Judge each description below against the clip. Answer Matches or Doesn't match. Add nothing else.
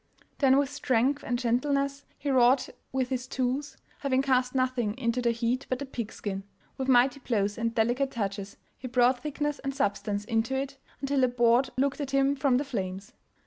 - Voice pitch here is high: Matches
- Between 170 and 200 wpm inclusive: Matches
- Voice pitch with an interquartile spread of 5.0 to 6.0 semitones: Doesn't match